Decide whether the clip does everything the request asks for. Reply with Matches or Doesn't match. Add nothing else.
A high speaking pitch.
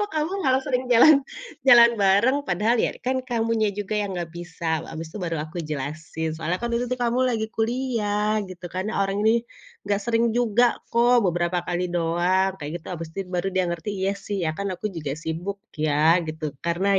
Matches